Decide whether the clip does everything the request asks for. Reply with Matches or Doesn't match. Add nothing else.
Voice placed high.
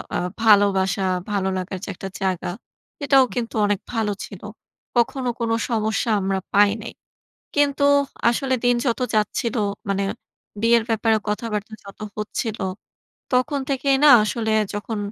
Matches